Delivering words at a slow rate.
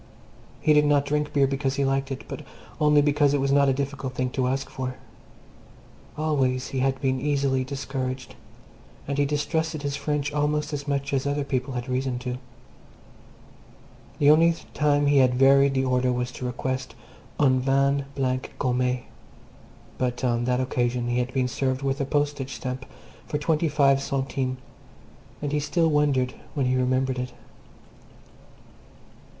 No: average, 165 wpm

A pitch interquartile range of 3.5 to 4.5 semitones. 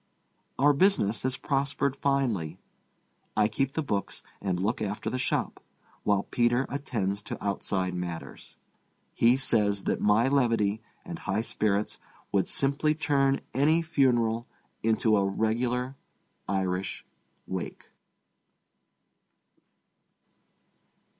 No: average, 5.3 semitones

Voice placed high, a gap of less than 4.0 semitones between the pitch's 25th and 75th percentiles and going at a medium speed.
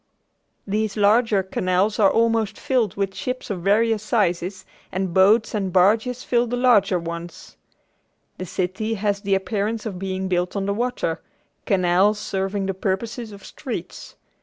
Yes: high, 200 Hz; average, 2.8 semitones; average, 150 wpm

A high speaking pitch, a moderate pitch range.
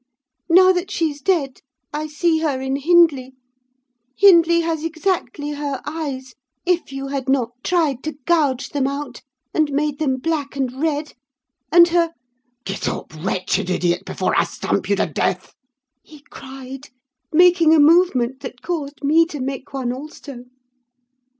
Yes: very high, 290 Hz; average, 3.7 semitones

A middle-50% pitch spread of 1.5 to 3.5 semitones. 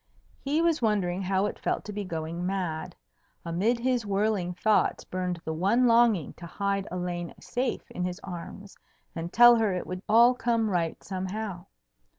No: average, 3.9 semitones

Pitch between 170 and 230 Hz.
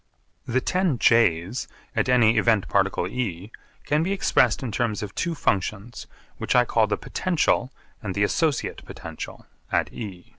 No: low, 115 Hz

